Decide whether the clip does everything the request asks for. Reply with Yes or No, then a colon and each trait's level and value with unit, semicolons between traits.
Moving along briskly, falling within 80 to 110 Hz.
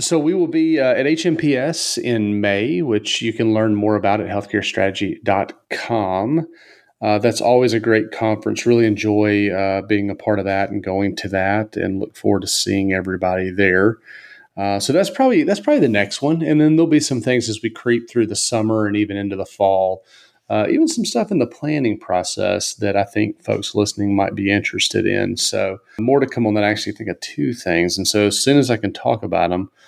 Yes: fast, 215 wpm; low, 105 Hz